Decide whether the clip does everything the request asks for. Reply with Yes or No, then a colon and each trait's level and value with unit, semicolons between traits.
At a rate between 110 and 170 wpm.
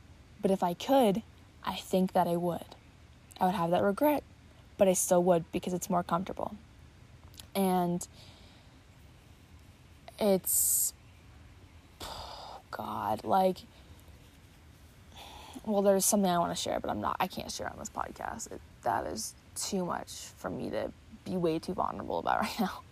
Yes: average, 150 wpm